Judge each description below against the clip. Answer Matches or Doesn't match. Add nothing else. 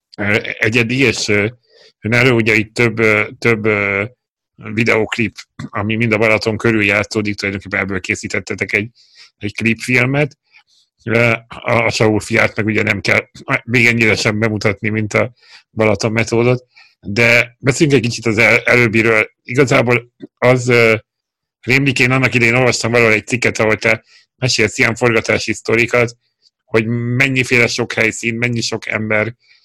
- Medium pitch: Doesn't match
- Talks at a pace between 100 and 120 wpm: Doesn't match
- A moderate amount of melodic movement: Doesn't match